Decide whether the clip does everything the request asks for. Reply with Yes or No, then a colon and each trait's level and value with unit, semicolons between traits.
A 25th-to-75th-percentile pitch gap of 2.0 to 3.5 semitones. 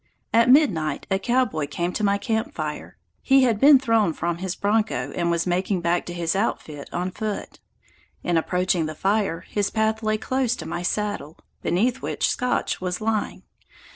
No: average, 4.4 semitones